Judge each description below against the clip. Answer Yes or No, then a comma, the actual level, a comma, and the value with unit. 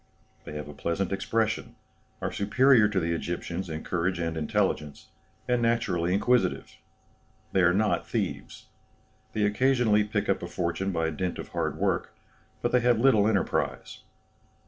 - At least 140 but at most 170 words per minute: Yes, average, 150 wpm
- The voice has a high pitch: No, very low, 95 Hz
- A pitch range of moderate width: Yes, average, 4.7 semitones